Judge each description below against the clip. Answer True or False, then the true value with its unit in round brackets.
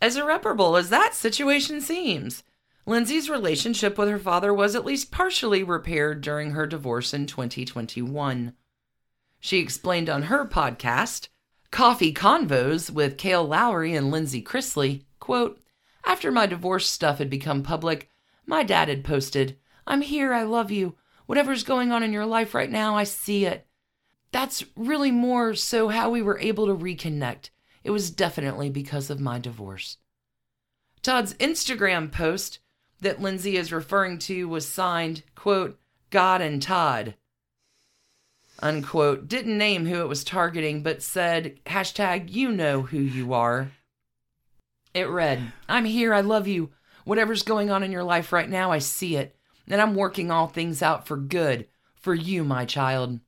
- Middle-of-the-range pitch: True (175 Hz)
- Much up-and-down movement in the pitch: True (6.9 semitones)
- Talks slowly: False (155 wpm)